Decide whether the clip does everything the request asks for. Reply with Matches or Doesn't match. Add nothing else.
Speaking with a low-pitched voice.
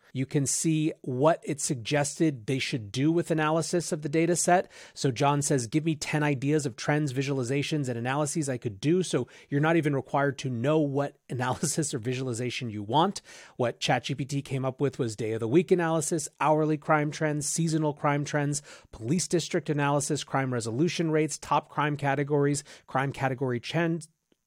Doesn't match